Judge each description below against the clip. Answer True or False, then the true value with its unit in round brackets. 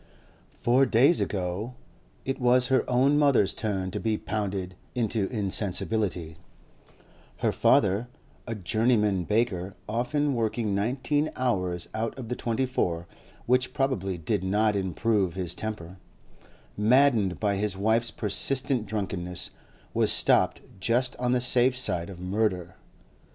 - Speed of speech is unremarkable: False (130 wpm)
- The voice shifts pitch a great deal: False (4.6 semitones)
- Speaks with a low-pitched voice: True (110 Hz)